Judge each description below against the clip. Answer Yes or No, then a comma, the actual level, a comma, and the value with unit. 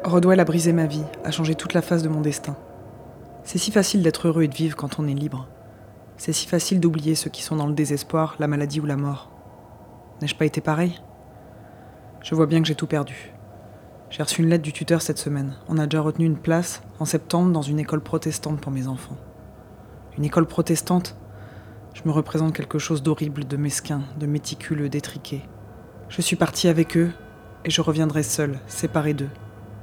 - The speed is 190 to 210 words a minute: Yes, average, 200 wpm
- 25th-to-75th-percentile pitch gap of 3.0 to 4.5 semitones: Yes, average, 3.7 semitones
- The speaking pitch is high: No, medium, 150 Hz